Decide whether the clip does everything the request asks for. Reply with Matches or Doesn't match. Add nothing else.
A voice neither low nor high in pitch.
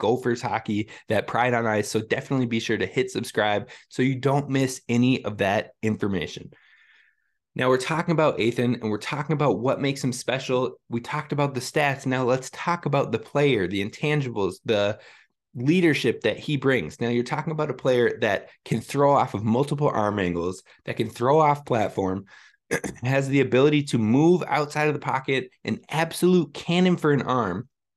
Doesn't match